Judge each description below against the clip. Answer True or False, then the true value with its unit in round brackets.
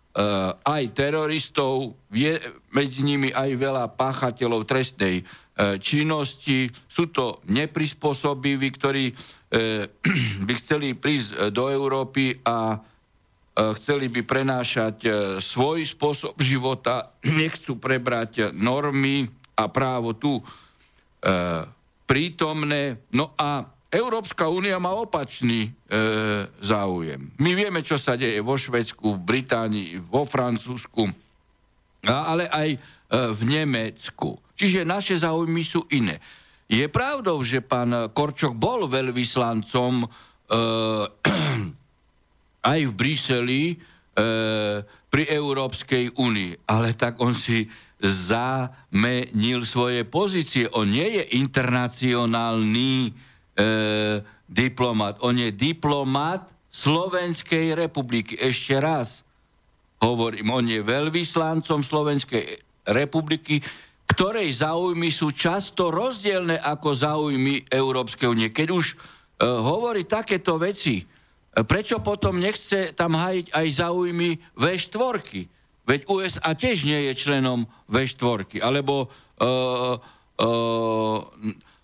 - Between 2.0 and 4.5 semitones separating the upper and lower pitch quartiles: False (5.0 semitones)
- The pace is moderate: False (100 wpm)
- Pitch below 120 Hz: False (130 Hz)